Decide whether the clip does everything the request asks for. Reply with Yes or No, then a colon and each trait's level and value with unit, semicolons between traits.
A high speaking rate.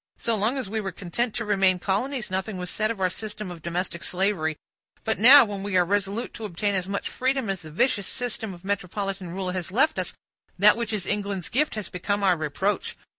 Yes: fast, 220 wpm